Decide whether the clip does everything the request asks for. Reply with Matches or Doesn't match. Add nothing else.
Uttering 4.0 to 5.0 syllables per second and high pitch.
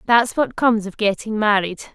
Doesn't match